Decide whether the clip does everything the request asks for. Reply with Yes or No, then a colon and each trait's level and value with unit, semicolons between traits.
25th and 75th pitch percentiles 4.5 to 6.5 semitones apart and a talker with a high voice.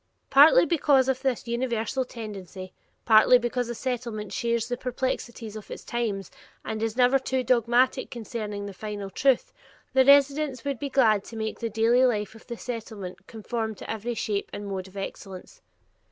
No: average, 3.2 semitones; high, 235 Hz